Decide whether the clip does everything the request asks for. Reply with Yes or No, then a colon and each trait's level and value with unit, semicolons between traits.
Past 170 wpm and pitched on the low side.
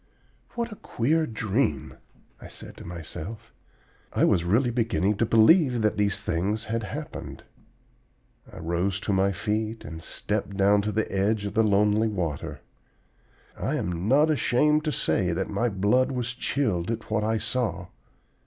No: average, 160 wpm; low, 105 Hz